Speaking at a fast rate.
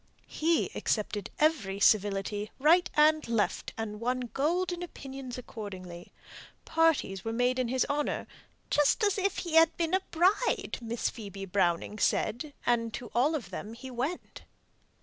No: average, 150 wpm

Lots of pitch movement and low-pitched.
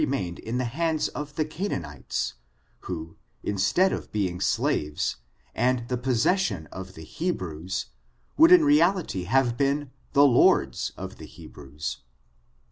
Yes: wide, 8.9 semitones; low, 120 Hz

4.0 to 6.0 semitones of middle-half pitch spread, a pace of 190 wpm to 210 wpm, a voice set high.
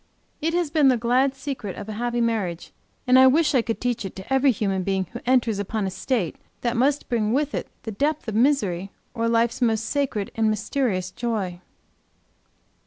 Yes: average, 4.3 semitones; average, 195 wpm; high, 235 Hz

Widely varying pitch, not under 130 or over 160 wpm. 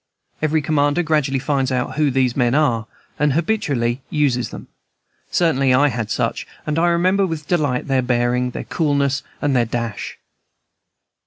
No: average, 3.6 semitones; average, 155 wpm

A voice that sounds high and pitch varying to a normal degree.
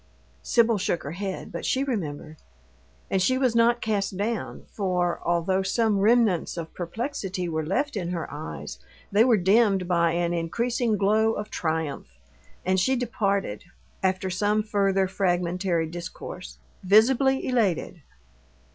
Yes: high, 195 Hz; average, 4.4 semitones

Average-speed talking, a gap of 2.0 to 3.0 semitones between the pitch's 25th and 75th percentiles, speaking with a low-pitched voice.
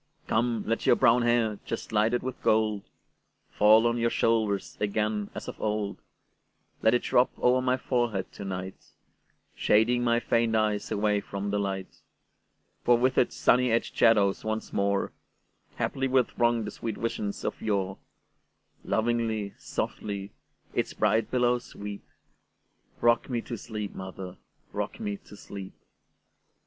No: slow, 125 wpm; narrow, 2.6 semitones; low, 110 Hz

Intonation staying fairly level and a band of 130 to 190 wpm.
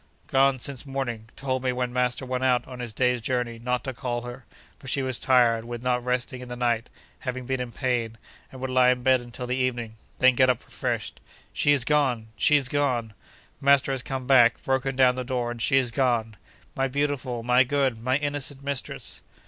No: narrow, 1.6 semitones; fast, 205 wpm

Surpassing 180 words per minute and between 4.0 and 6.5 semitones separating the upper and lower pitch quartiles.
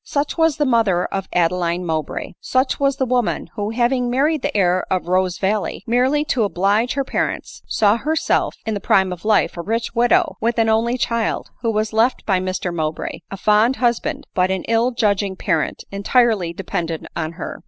Yes: average, 190 wpm; average, 4.7 semitones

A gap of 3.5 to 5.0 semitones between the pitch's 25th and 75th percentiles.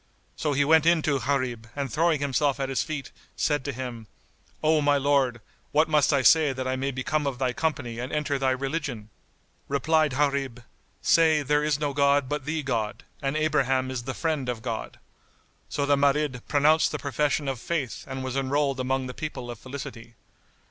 No: narrow, 2.5 semitones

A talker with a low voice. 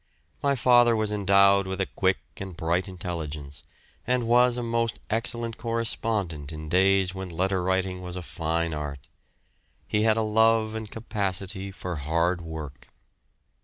Yes: very low, 95 Hz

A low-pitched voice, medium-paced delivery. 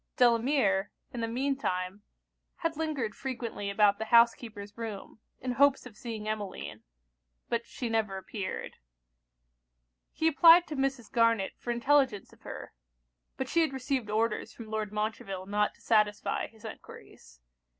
No: high, 230 Hz; average, 145 wpm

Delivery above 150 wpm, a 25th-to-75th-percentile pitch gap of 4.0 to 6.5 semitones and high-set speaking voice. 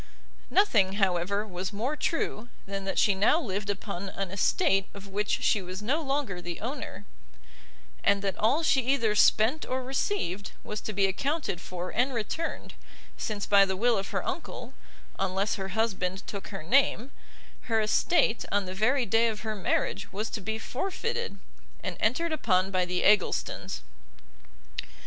Yes: average, 165 wpm; average, 4.4 semitones; high, 210 Hz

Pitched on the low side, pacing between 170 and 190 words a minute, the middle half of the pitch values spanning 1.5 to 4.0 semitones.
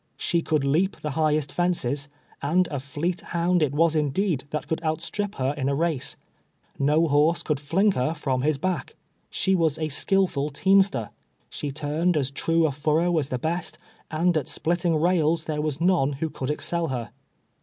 No: medium, 155 Hz; average, 175 wpm; average, 3.1 semitones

